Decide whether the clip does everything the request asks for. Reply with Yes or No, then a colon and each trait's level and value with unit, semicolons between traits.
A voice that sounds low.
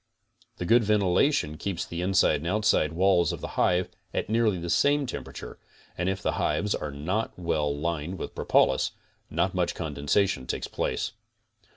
Yes: very low, 90 Hz